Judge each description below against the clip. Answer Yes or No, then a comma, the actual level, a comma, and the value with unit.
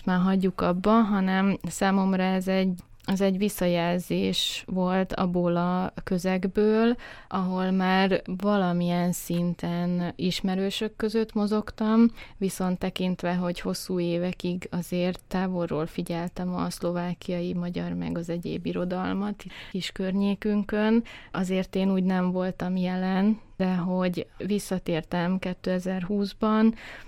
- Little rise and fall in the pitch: Yes, narrow, 1.7 semitones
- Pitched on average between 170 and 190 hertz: Yes, medium, 185 Hz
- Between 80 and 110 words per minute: Yes, slow, 105 wpm